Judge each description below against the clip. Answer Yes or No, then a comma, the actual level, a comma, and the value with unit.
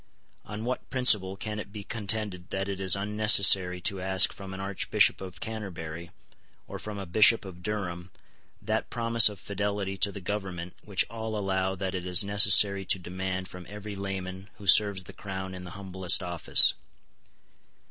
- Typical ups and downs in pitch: No, narrow, 2.0 semitones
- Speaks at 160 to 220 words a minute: Yes, average, 170 wpm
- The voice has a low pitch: Yes, very low, 95 Hz